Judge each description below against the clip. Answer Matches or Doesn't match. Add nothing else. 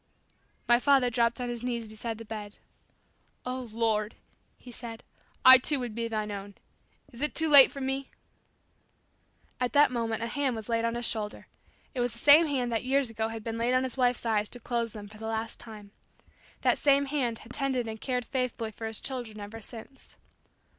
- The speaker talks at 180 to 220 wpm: Matches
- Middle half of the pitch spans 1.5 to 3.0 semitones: Matches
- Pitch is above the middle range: Matches